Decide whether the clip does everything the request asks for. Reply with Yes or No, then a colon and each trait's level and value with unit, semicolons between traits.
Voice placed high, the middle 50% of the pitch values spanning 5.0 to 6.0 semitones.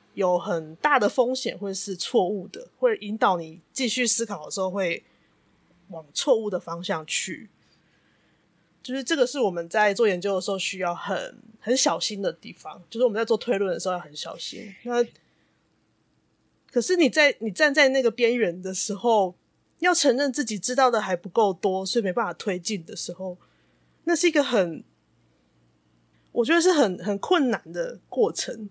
Yes: high, 210 Hz; average, 5.3 semitones